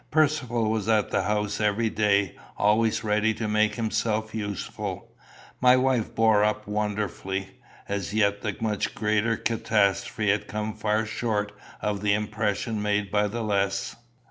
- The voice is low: Yes, low, 105 Hz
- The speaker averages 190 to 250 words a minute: No, average, 145 wpm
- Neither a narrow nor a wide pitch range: No, narrow, 1.2 semitones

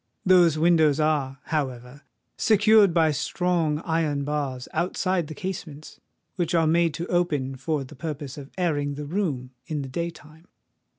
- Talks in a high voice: No, medium, 155 Hz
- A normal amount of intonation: Yes, average, 3.2 semitones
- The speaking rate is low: No, average, 155 wpm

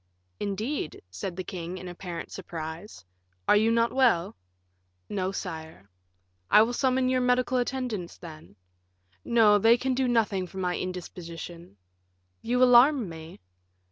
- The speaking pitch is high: Yes, high, 195 Hz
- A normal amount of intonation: No, wide, 6.1 semitones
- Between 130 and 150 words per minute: Yes, average, 140 wpm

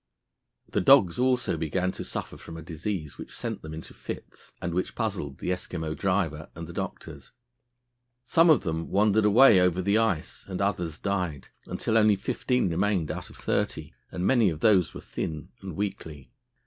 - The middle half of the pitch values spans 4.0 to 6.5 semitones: Yes, average, 4.3 semitones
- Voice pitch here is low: Yes, very low, 90 Hz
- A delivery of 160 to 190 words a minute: Yes, average, 175 wpm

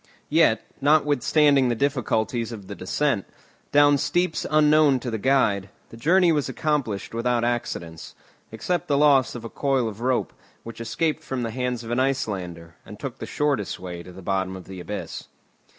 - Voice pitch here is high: No, low, 125 Hz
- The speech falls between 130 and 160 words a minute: No, average, 175 wpm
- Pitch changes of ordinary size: No, wide, 5.8 semitones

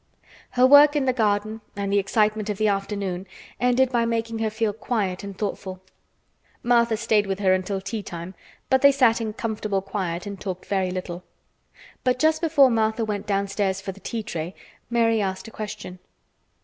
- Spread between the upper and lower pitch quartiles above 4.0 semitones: No, average, 2.9 semitones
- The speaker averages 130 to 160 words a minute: No, average, 180 wpm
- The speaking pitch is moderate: No, high, 210 Hz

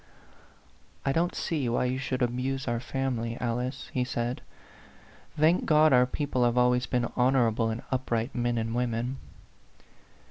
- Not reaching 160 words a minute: Yes, average, 150 wpm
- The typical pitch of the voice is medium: No, low, 125 Hz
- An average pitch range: No, narrow, 2.0 semitones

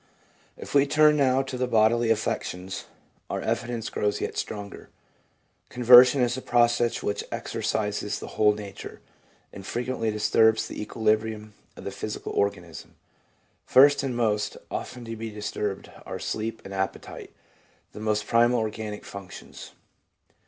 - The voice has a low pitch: Yes, low, 110 Hz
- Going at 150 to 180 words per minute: No, average, 140 wpm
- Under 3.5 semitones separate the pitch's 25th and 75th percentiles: Yes, narrow, 2.6 semitones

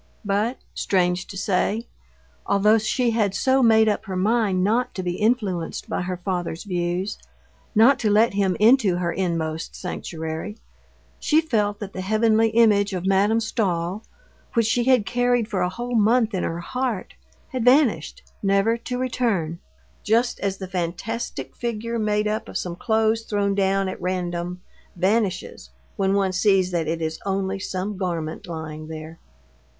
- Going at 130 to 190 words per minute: Yes, average, 160 wpm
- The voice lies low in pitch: No, high, 200 Hz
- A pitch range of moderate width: Yes, average, 3.9 semitones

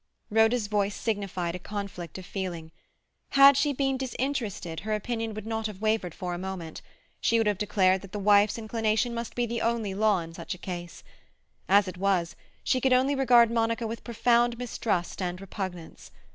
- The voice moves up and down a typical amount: Yes, average, 4.0 semitones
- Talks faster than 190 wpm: No, average, 185 wpm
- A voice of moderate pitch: No, high, 210 Hz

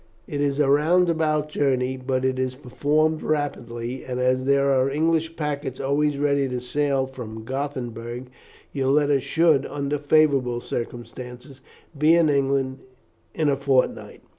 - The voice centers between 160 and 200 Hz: No, medium, 140 Hz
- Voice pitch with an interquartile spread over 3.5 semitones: No, narrow, 2.4 semitones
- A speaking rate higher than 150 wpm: No, average, 145 wpm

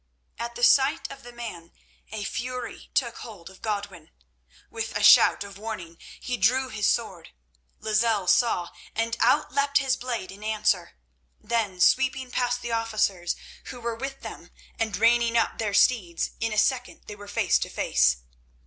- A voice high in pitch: Yes, high, 225 Hz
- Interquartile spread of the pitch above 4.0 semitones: No, average, 3.4 semitones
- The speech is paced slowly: No, average, 165 wpm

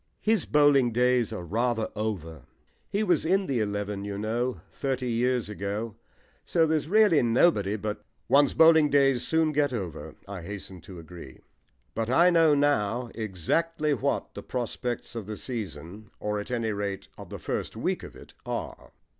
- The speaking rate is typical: Yes, average, 170 wpm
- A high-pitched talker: No, low, 120 Hz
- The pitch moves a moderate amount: No, wide, 6.0 semitones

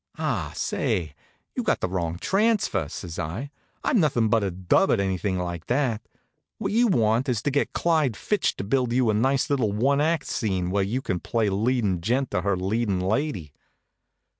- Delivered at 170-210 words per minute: Yes, average, 190 wpm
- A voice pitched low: Yes, low, 110 Hz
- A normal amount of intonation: No, wide, 6.5 semitones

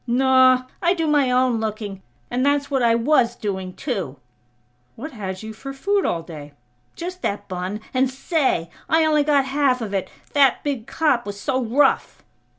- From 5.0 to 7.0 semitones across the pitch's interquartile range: Yes, wide, 5.5 semitones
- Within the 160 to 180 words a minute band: Yes, average, 175 wpm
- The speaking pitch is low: No, very high, 255 Hz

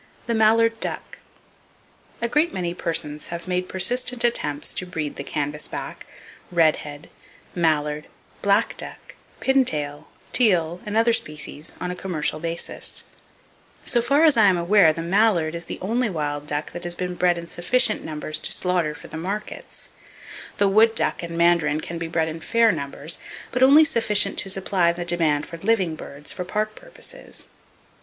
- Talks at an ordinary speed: Yes, average, 165 wpm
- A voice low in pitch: No, medium, 175 Hz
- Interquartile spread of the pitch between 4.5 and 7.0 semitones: Yes, wide, 5.4 semitones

